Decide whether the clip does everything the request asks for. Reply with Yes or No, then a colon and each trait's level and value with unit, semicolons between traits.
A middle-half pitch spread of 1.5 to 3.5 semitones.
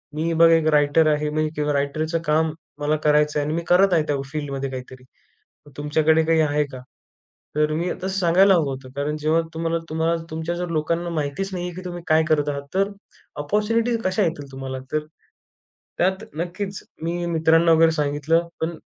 Yes: narrow, 2.5 semitones